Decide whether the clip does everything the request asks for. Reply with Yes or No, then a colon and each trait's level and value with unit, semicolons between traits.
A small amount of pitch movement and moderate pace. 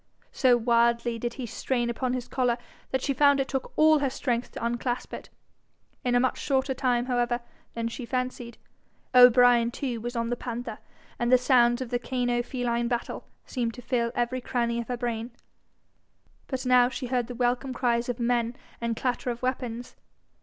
Yes: narrow, 1.3 semitones; average, 180 wpm